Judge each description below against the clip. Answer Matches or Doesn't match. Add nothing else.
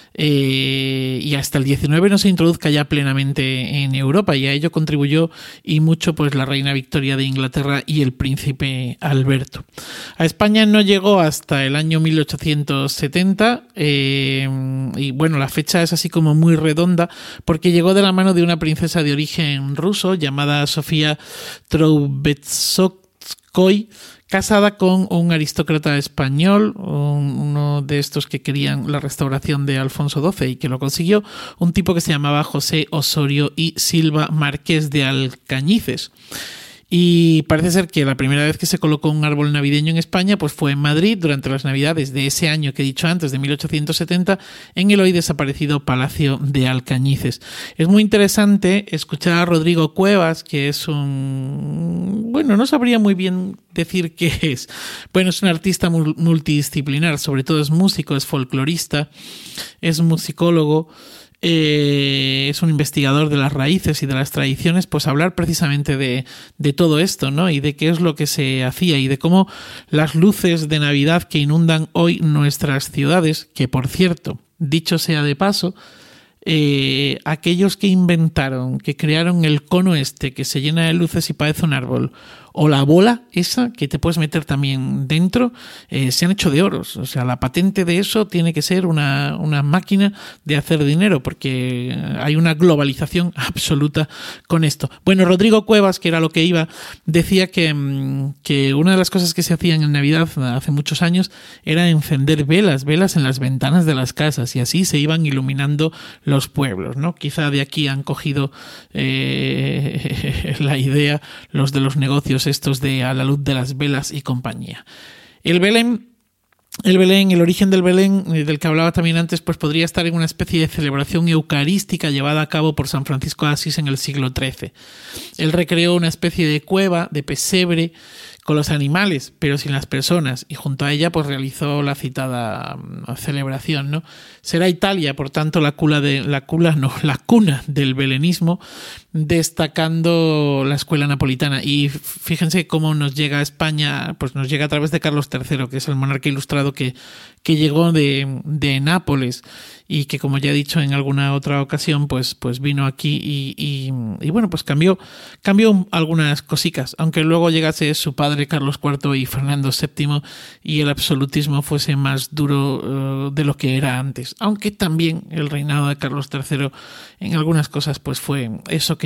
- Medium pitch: Matches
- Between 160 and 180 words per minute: Matches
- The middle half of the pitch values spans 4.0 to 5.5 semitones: Doesn't match